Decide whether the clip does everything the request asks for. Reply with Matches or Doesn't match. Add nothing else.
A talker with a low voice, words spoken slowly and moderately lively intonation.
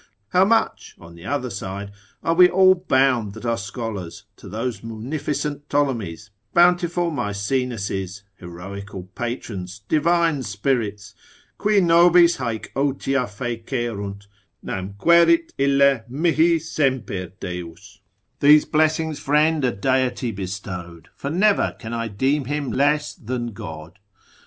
Doesn't match